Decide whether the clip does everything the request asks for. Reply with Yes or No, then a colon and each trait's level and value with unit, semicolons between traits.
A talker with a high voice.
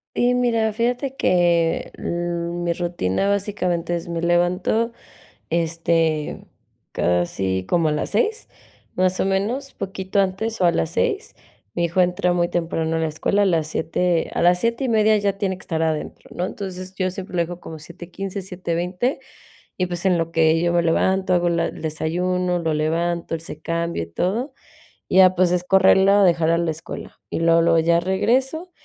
No: medium, 175 Hz